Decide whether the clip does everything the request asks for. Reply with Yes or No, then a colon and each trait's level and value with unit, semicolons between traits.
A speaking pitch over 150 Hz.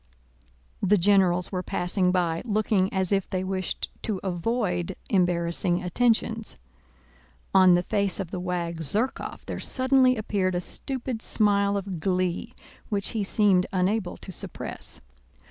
Yes: high, 190 Hz